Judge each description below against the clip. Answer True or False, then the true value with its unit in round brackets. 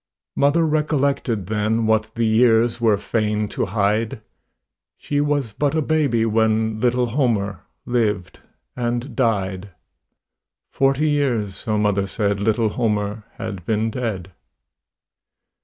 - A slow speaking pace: True (120 wpm)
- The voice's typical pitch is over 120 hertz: False (110 Hz)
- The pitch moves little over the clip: False (3.1 semitones)